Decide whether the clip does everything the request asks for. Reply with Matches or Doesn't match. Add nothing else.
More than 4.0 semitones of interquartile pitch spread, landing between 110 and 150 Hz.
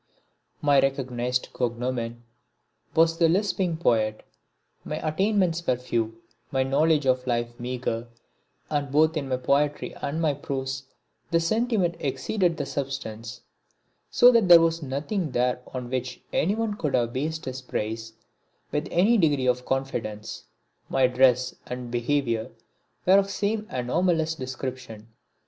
Matches